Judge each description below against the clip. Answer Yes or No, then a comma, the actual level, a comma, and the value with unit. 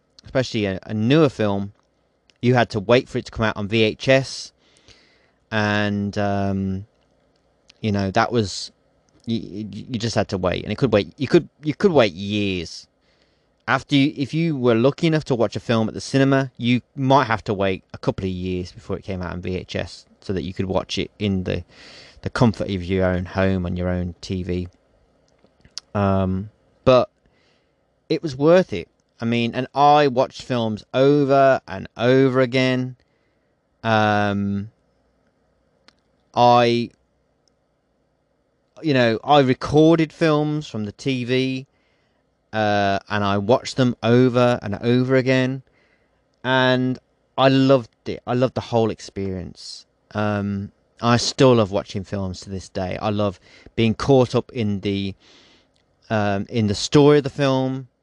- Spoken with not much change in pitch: No, average, 4.8 semitones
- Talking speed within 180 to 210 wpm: No, average, 155 wpm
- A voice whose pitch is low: Yes, low, 110 Hz